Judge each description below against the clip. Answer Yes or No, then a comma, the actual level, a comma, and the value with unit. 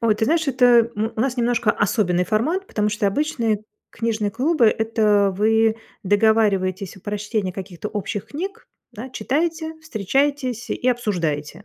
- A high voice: Yes, high, 220 Hz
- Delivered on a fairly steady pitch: No, average, 3.6 semitones